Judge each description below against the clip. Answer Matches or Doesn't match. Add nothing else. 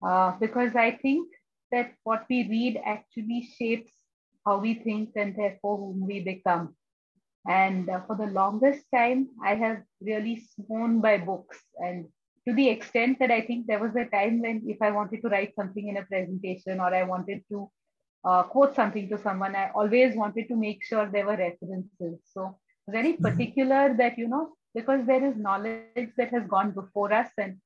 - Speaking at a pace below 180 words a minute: Doesn't match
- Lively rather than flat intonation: Doesn't match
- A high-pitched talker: Matches